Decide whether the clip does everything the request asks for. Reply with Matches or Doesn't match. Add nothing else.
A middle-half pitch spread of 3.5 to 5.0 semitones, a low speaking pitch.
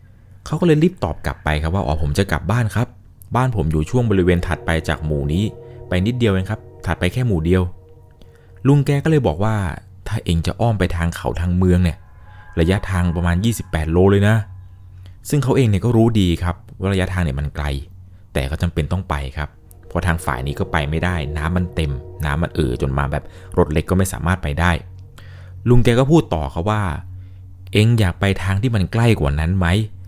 Matches